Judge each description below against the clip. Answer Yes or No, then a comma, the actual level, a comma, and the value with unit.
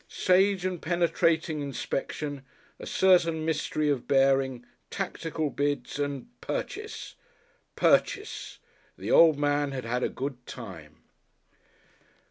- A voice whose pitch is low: No, medium, 145 Hz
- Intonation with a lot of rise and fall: No, average, 3.8 semitones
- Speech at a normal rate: No, slow, 105 wpm